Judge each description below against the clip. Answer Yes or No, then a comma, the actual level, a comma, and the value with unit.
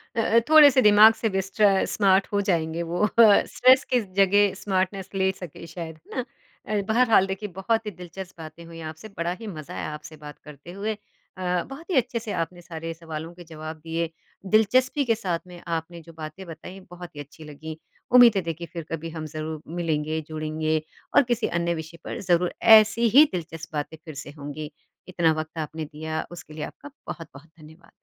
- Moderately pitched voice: Yes, medium, 175 Hz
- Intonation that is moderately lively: Yes, average, 4.5 semitones